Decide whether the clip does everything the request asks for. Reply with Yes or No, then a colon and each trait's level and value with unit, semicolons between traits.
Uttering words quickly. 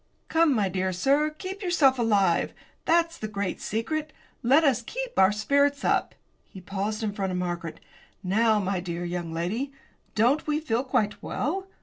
No: average, 165 wpm